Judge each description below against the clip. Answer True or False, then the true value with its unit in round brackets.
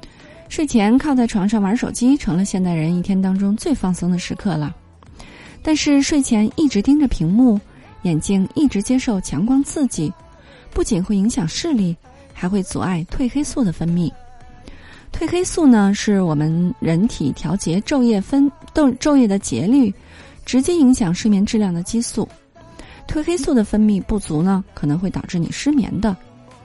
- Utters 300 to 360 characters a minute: False (250 characters per minute)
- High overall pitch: True (210 Hz)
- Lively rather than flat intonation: True (6.6 semitones)